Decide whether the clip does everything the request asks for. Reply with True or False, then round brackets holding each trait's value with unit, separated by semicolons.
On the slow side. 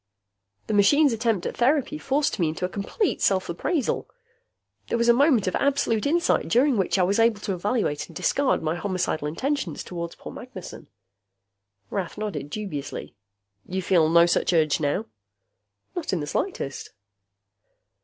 False (155 wpm)